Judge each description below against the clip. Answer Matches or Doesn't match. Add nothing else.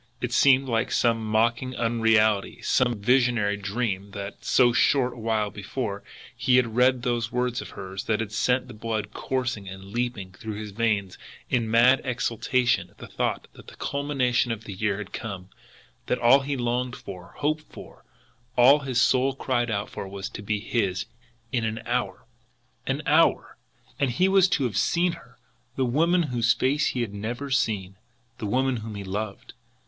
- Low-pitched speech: Matches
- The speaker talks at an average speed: Matches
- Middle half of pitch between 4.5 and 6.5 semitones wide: Doesn't match